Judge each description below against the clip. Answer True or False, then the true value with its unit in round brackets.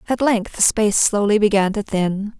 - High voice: True (205 Hz)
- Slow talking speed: False (200 wpm)